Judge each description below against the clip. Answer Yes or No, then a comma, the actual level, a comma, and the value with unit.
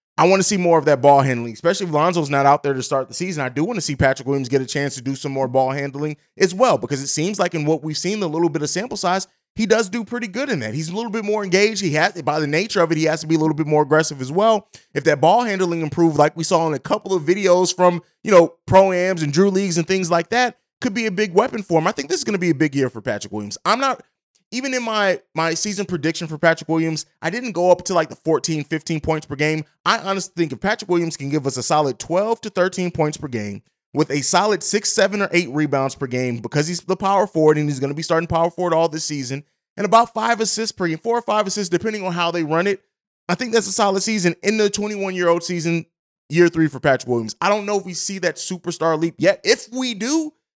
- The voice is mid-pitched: Yes, medium, 170 Hz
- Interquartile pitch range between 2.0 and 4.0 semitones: No, average, 4.5 semitones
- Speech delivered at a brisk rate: Yes, fast, 285 wpm